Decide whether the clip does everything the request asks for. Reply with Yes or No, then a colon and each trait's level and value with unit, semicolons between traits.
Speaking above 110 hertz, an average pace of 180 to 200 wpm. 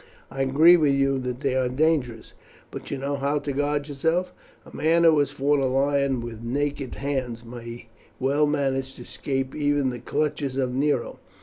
Yes: medium, 140 Hz; average, 185 wpm